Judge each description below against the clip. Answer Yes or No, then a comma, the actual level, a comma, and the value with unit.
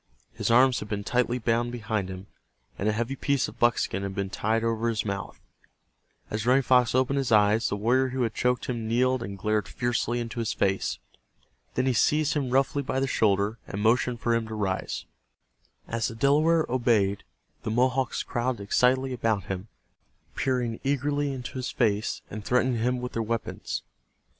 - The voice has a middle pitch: No, low, 120 Hz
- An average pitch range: Yes, average, 3.0 semitones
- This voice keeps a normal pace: Yes, average, 180 wpm